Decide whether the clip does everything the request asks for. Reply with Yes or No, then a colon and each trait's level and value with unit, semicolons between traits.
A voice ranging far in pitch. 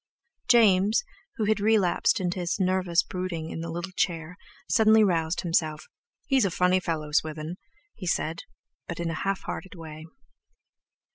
No: average, 3.0 semitones